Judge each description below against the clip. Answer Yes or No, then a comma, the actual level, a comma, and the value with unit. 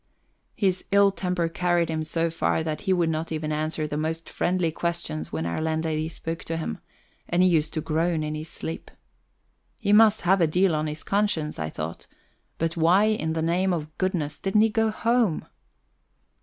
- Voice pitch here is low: No, medium, 165 Hz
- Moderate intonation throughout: Yes, average, 3.0 semitones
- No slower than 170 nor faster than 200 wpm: Yes, average, 190 wpm